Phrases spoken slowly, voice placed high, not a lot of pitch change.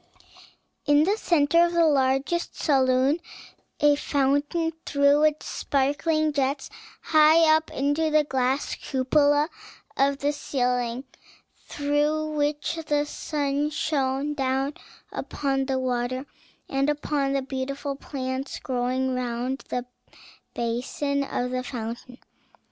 Yes: slow, 115 wpm; very high, 280 Hz; narrow, 2.2 semitones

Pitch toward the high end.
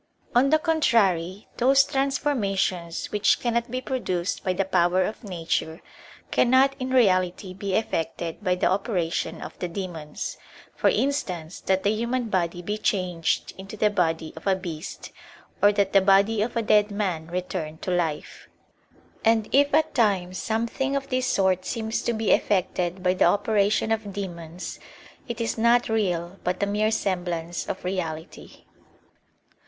Yes: high, 195 Hz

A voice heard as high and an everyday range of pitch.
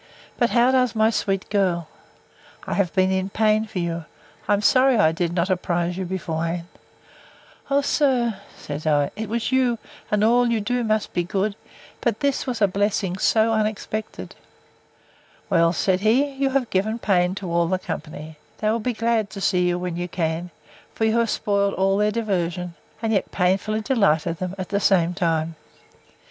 Yes: high, 195 Hz; average, 4.0 semitones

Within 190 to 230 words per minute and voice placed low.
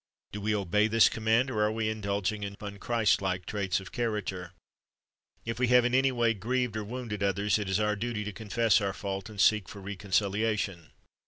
Yes: average, 195 wpm; low, 105 Hz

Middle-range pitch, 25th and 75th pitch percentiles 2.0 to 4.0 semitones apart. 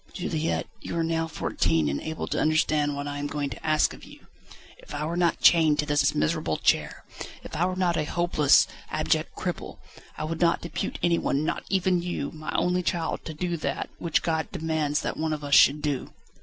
Yes: medium, 155 Hz; narrow, 2.5 semitones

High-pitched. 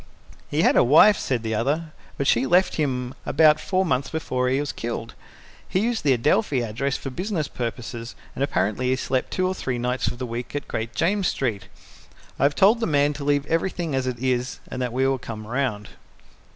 No: low, 135 Hz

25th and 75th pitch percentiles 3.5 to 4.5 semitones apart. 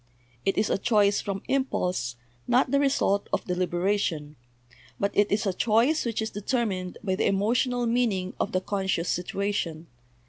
Yes: average, 3.9 semitones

